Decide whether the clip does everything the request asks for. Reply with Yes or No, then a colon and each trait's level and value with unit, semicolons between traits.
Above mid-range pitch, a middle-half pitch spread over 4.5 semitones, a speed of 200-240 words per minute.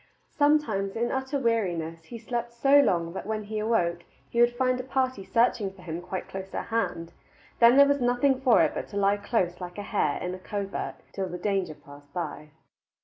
Yes: high, 210 Hz; average, 5.1 semitones; fast, 205 wpm